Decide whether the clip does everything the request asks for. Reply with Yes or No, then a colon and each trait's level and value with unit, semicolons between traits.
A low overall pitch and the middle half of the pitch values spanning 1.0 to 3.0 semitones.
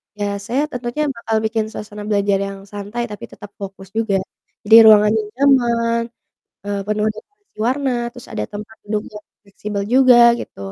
No: high, 215 Hz; average, 2.7 semitones